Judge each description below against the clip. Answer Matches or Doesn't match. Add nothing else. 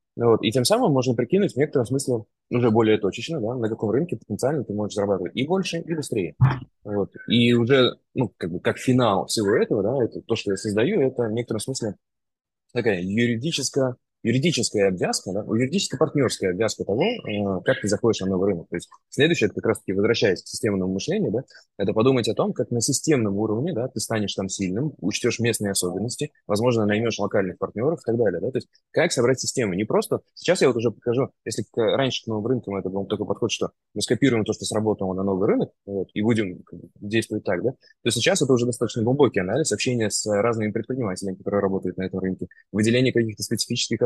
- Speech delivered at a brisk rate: Matches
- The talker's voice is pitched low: Matches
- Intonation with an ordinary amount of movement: Matches